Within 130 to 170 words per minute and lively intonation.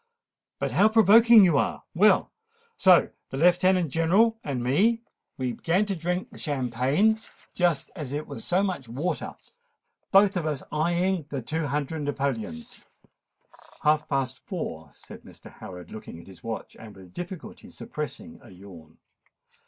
Yes: average, 150 wpm; wide, 6.7 semitones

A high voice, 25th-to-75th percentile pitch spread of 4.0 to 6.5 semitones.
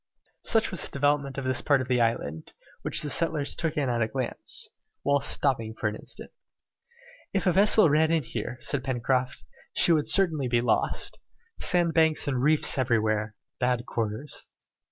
No: low, 135 Hz; average, 4.5 semitones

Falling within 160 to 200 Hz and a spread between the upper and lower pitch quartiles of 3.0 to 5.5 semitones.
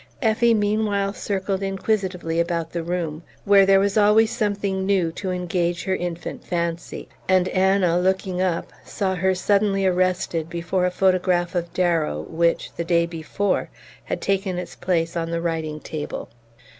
No: medium, 185 Hz; narrow, 2.5 semitones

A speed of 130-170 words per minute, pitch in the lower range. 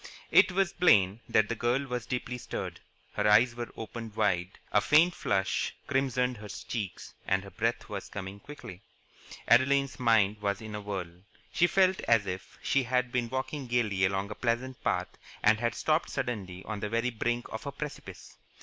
No: average, 180 wpm; low, 115 Hz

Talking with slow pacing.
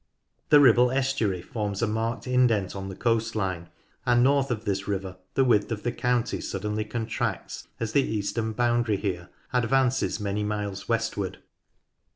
No: average, 160 wpm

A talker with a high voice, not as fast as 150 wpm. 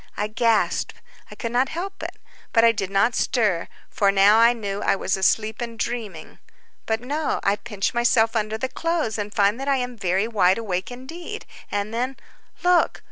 No: high, 225 Hz; average, 175 wpm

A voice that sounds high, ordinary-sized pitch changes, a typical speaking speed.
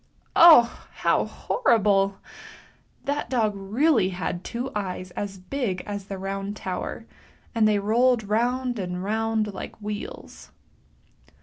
No: high, 210 Hz; average, 3.4 semitones; slow, 125 wpm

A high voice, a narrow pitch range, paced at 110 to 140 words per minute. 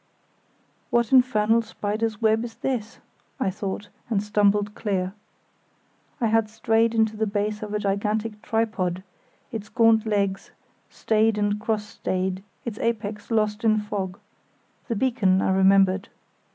Yes: high, 210 Hz; narrow, 1.9 semitones; slow, 135 wpm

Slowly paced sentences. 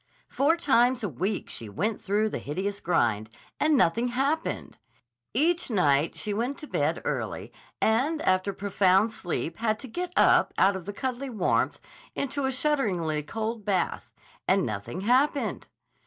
No: average, 150 wpm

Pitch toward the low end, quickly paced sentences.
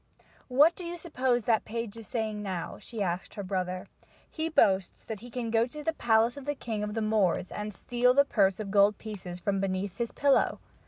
No: high, 220 Hz; fast, 215 wpm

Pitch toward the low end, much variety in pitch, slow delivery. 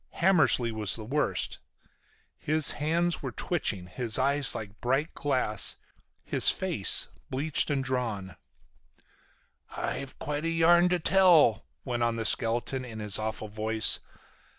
Yes: low, 130 Hz; wide, 5.8 semitones; slow, 130 wpm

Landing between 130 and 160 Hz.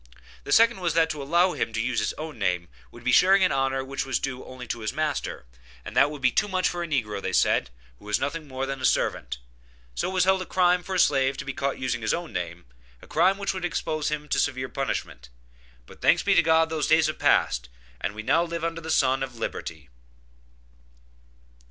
Yes: medium, 140 Hz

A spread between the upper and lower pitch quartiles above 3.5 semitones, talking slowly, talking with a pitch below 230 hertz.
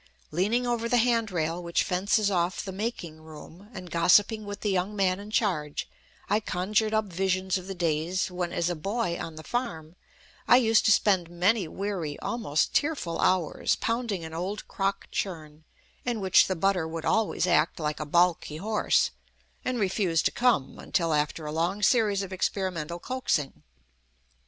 No: average, 4.1 semitones; average, 170 wpm; medium, 185 Hz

